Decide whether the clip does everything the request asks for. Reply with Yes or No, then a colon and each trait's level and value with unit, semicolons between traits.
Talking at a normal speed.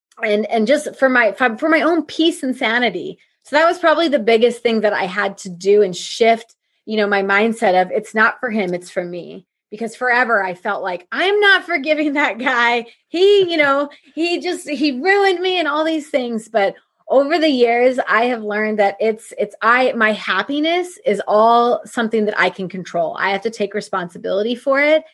No: fast, 210 wpm